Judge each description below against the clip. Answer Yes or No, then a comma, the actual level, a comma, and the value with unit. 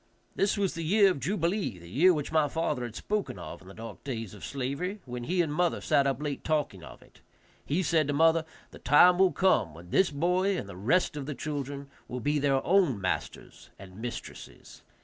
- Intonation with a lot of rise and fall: Yes, wide, 6.3 semitones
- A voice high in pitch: No, medium, 145 Hz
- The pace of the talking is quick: Yes, fast, 215 wpm